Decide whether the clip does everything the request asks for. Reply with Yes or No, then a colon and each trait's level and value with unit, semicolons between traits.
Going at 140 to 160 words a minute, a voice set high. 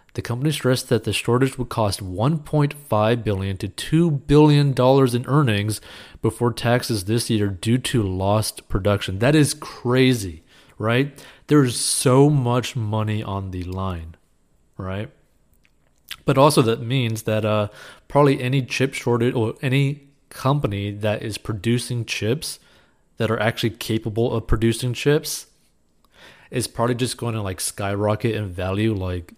No: average, 145 wpm; low, 115 Hz